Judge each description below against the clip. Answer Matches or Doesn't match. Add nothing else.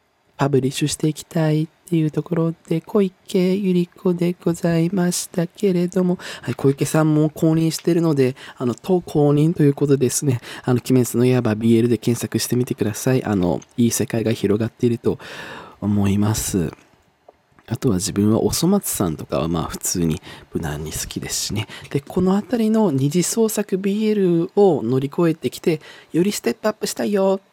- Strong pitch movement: Matches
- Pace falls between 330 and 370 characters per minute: Matches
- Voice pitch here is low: Doesn't match